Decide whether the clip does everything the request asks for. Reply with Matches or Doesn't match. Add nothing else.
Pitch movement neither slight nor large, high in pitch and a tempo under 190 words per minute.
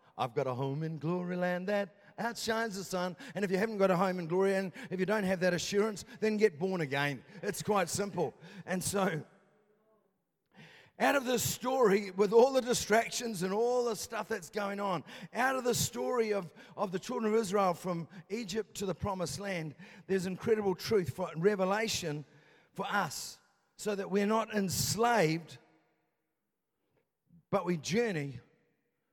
Matches